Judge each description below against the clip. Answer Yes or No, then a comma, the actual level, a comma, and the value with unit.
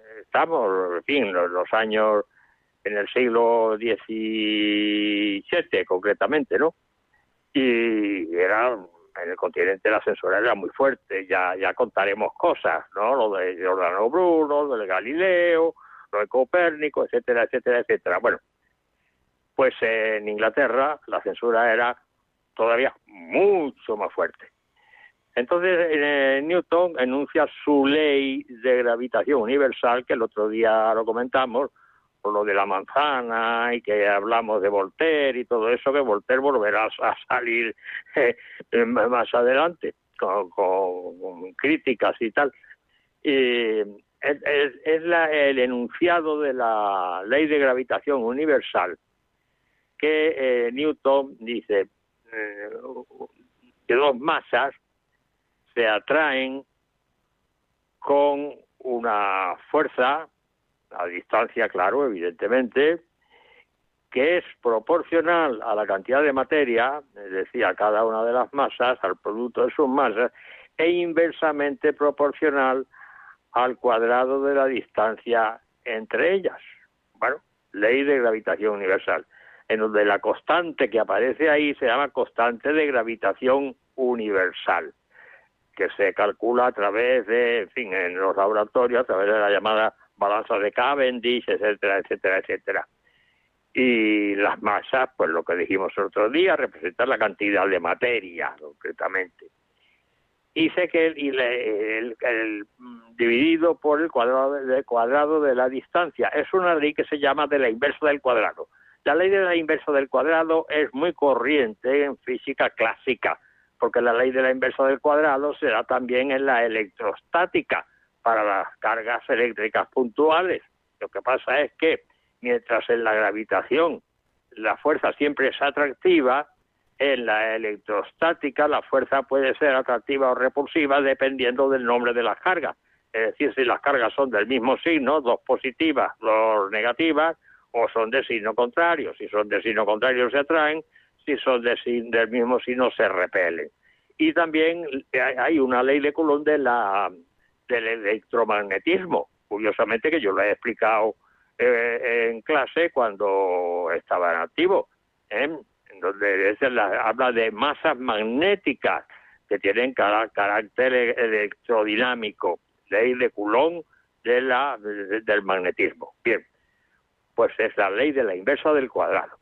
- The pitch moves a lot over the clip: Yes, wide, 6.4 semitones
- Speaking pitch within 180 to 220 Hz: No, low, 135 Hz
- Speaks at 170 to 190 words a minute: No, average, 140 wpm